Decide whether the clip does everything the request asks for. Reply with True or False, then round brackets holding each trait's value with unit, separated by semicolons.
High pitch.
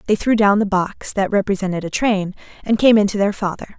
True (200 Hz)